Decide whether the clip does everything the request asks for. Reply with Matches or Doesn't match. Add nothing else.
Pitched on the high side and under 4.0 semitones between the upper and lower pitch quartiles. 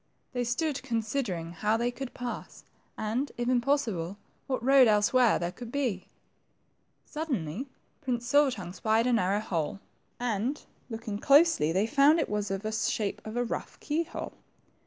Doesn't match